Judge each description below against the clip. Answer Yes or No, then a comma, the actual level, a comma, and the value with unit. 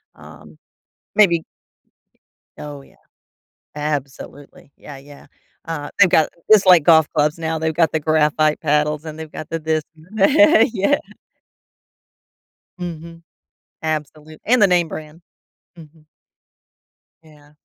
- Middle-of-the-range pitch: Yes, medium, 155 Hz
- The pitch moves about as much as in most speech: No, narrow, 1.9 semitones